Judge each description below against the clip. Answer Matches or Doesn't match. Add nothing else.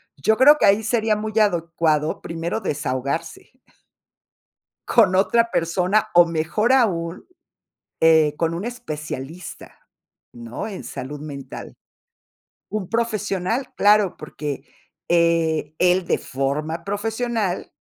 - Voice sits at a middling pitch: Matches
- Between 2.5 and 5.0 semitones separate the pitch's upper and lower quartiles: Doesn't match